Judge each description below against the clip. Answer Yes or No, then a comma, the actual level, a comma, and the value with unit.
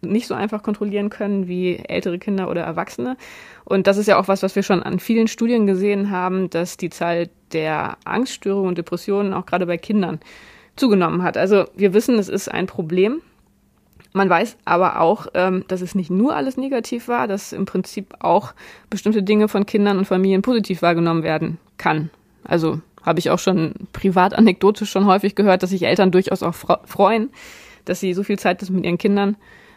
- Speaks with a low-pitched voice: No, high, 195 Hz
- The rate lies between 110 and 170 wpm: No, average, 185 wpm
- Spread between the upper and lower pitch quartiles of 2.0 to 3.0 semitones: Yes, narrow, 2.5 semitones